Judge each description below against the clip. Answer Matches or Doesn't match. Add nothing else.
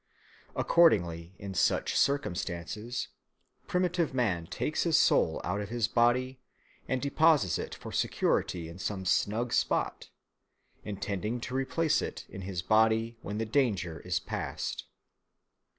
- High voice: Doesn't match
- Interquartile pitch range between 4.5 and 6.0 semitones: Matches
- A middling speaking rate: Doesn't match